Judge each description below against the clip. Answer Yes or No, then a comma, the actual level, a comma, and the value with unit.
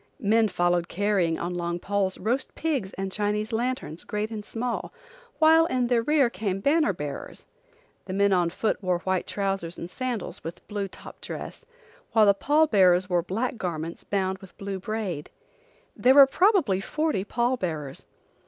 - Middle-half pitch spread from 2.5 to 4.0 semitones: No, average, 4.8 semitones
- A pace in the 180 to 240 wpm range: No, average, 165 wpm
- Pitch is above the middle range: Yes, high, 200 Hz